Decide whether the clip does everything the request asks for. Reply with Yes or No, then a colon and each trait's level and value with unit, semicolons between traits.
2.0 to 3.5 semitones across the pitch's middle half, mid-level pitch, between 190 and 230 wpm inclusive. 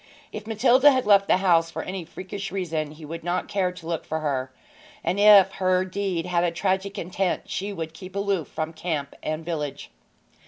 Yes: average, 3.2 semitones; medium, 180 Hz; average, 195 wpm